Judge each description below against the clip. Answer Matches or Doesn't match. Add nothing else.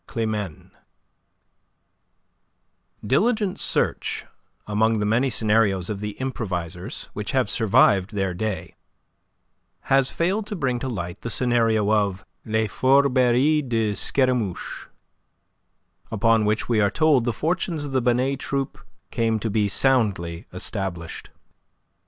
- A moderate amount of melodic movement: Matches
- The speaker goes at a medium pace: Doesn't match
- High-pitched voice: Doesn't match